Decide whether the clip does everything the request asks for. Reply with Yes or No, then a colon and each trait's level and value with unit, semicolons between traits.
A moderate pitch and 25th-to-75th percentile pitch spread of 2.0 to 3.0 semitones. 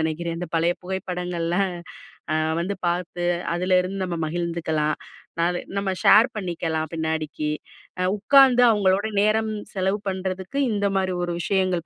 Yes: medium, 180 Hz; narrow, 2.6 semitones